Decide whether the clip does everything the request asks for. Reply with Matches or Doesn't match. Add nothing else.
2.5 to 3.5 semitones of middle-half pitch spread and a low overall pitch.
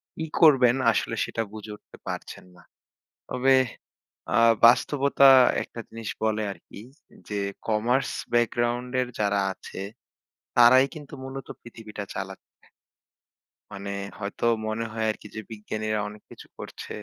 Matches